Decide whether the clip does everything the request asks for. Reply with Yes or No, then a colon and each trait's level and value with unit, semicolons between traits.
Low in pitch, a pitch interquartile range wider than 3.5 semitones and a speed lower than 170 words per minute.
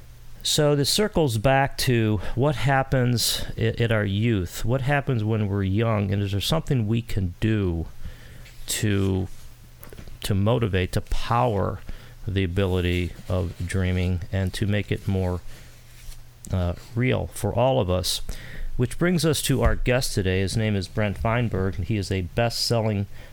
Yes: low, 105 Hz; average, 4.2 semitones; average, 155 wpm